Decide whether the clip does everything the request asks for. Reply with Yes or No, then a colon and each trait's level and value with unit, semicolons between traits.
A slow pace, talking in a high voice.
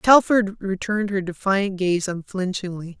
Yes: slow, 120 wpm; high, 195 Hz